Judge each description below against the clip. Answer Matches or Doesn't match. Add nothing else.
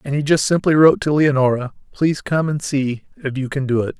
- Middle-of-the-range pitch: Matches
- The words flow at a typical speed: Doesn't match